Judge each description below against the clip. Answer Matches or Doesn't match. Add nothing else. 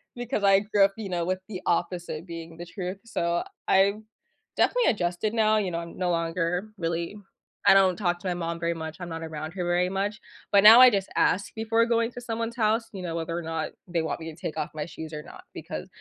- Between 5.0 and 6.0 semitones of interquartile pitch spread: Doesn't match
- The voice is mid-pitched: Matches